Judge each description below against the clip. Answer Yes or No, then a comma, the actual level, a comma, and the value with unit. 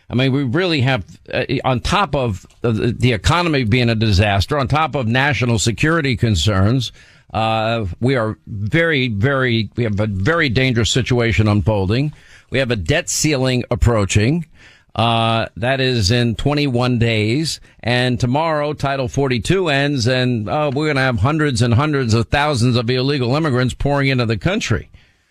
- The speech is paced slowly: No, average, 160 wpm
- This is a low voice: Yes, low, 125 Hz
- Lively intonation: No, average, 3.8 semitones